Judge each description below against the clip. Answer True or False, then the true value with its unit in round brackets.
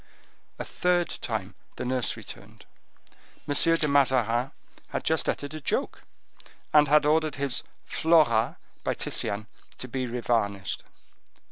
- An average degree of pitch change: True (4.5 semitones)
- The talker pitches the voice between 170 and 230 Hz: False (135 Hz)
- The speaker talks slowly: True (125 wpm)